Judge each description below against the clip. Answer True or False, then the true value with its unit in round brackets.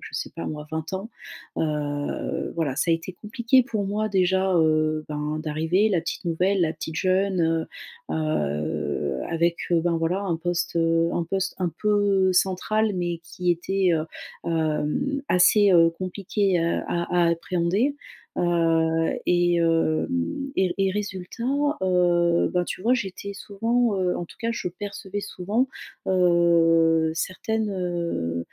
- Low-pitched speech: False (175 Hz)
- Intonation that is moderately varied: True (3.1 semitones)